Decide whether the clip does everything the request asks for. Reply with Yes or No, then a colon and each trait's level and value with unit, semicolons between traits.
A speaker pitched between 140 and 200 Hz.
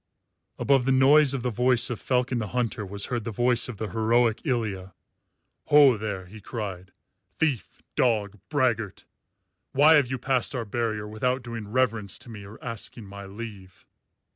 No: low, 115 Hz